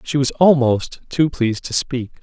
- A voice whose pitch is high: No, low, 130 Hz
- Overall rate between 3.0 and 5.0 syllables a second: Yes, 4.4 syllables/s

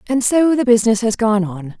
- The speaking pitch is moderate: No, high, 230 Hz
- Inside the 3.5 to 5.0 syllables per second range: No, 5.4 syllables/s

